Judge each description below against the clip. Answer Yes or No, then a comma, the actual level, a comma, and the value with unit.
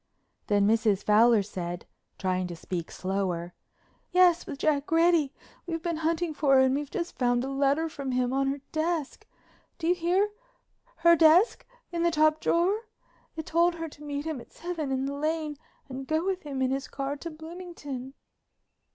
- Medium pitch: No, very high, 295 Hz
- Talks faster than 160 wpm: Yes, average, 175 wpm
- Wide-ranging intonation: No, average, 4.4 semitones